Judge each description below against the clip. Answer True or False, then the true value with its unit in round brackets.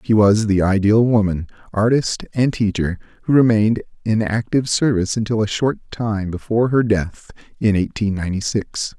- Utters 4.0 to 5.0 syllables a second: False (5.2 syllables/s)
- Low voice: True (105 Hz)